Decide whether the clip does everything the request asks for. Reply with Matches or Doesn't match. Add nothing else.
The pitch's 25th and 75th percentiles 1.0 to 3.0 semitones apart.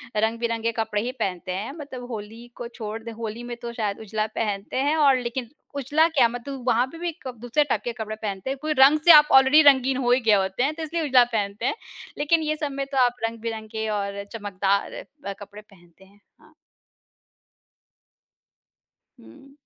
Doesn't match